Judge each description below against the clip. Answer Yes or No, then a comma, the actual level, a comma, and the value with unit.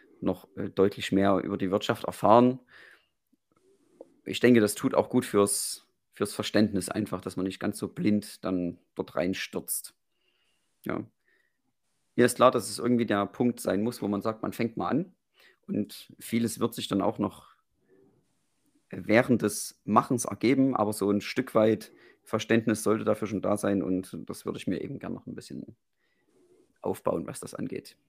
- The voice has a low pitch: Yes, low, 105 Hz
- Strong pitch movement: No, average, 2.9 semitones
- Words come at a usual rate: Yes, average, 170 wpm